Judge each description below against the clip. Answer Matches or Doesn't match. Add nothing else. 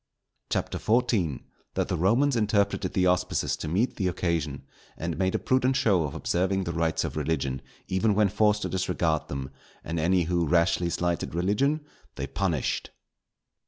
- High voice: Doesn't match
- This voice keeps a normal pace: Matches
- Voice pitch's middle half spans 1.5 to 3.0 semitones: Doesn't match